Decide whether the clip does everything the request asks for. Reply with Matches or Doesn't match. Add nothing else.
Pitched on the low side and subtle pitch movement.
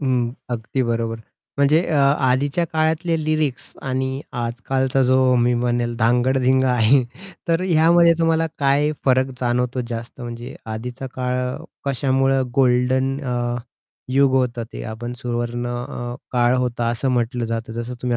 Matches